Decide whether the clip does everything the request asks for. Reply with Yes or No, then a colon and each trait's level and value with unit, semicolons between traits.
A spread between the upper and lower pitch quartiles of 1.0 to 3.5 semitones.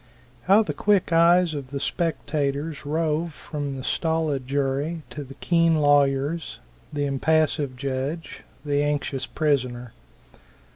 Yes: average, 2.9 semitones